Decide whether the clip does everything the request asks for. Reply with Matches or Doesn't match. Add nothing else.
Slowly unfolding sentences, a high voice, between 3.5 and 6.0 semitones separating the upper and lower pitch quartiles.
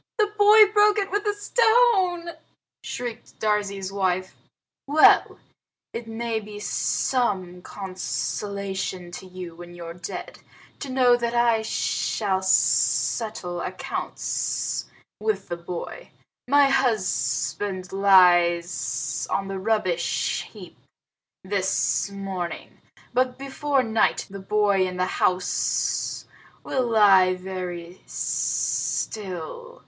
Matches